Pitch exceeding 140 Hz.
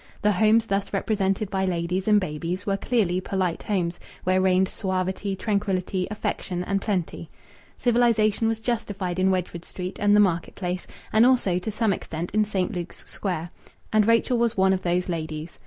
Yes: high, 190 Hz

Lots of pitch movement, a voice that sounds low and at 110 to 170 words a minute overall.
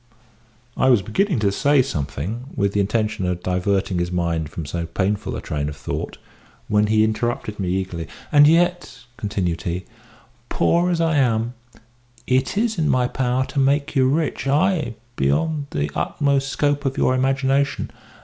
Yes: wide, 7.3 semitones; low, 120 Hz; average, 165 wpm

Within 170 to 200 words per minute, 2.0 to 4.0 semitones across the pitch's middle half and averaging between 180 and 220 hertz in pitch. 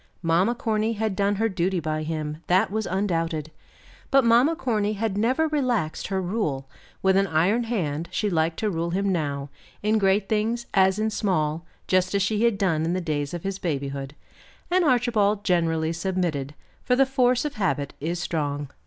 No: average, 180 wpm; average, 5.3 semitones; high, 190 Hz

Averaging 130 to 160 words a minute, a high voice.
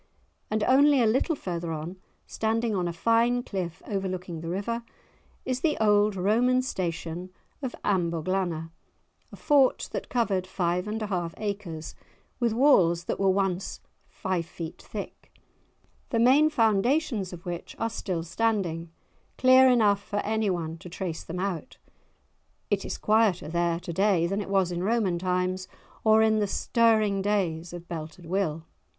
Yes: average, 155 wpm; high, 195 Hz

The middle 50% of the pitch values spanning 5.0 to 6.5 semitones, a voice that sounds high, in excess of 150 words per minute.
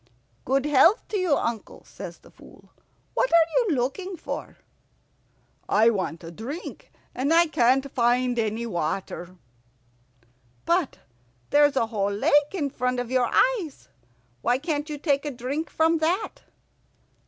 No: wide, 5.5 semitones; very high, 275 Hz; average, 140 wpm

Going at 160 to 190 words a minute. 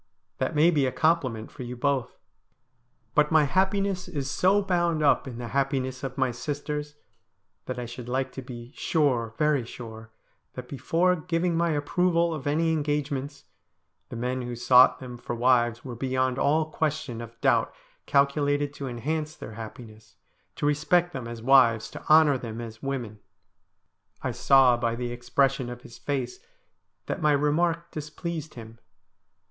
Yes: average, 165 wpm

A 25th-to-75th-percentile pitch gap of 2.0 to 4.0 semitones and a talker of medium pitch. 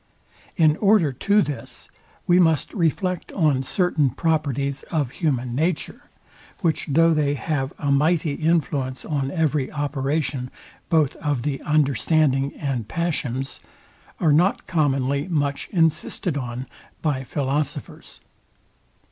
Yes: average, 3.0 semitones; medium, 150 Hz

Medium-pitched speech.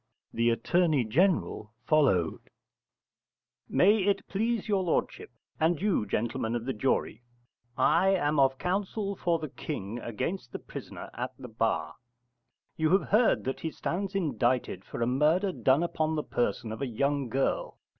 Yes: medium, 150 Hz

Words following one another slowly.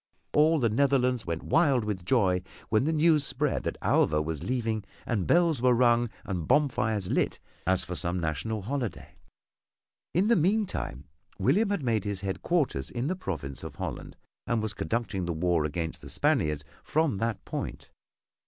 No: average, 165 wpm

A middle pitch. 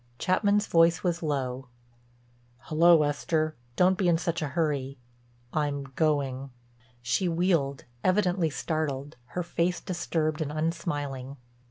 Yes: medium, 155 Hz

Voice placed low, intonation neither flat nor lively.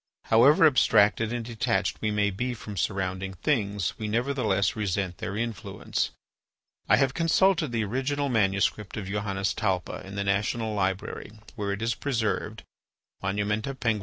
Yes: low, 105 Hz; average, 3.4 semitones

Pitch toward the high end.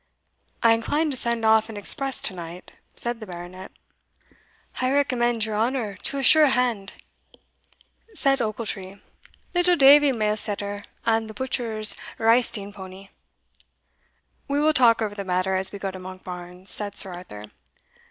Yes: high, 220 Hz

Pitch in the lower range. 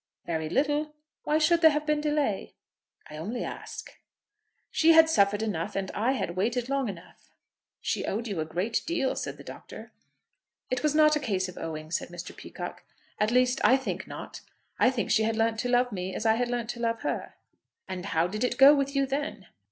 No: high, 240 Hz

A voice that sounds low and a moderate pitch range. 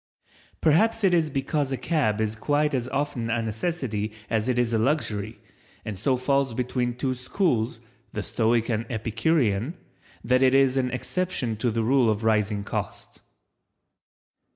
Yes: low, 125 Hz; average, 3.8 semitones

